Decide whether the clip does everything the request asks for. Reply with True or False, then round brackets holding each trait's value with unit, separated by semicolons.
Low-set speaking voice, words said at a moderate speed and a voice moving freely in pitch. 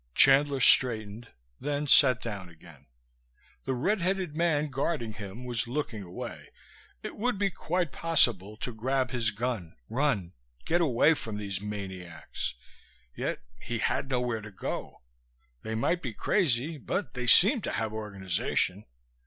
True (120 Hz; 145 wpm; 5.9 semitones)